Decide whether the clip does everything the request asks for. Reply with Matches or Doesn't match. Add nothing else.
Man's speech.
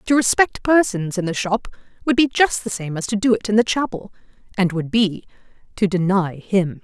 Doesn't match